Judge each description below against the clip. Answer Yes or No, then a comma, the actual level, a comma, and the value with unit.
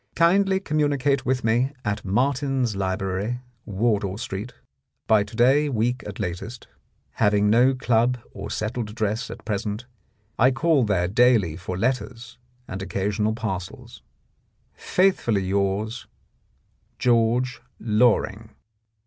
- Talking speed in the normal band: No, slow, 115 wpm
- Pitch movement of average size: Yes, average, 3.8 semitones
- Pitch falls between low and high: No, low, 115 Hz